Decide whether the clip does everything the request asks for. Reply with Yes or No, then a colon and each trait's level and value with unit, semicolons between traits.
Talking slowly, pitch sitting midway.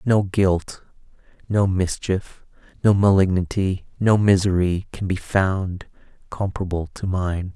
No: slow, 110 wpm; very low, 95 Hz